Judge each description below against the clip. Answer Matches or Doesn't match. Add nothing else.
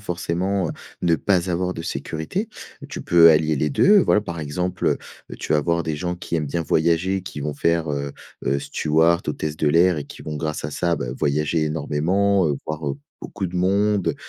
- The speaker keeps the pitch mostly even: Doesn't match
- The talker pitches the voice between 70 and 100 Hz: Matches